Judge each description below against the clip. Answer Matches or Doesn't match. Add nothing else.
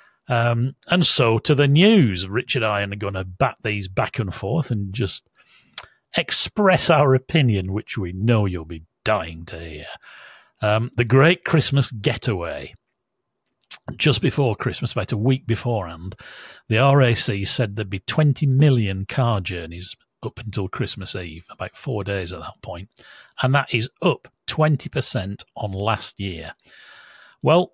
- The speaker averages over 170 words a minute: Doesn't match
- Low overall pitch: Matches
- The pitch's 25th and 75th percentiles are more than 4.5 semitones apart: Matches